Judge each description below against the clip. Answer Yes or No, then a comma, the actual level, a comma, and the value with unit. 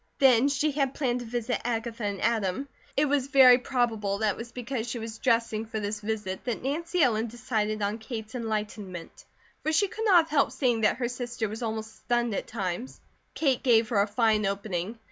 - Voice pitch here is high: Yes, high, 230 Hz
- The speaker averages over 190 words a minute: Yes, average, 200 wpm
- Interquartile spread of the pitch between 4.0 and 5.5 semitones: No, average, 2.9 semitones